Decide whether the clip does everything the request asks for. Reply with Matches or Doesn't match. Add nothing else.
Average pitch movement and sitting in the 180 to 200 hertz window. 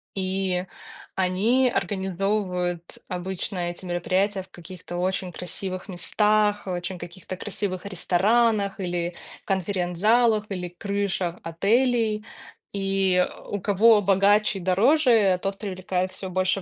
Doesn't match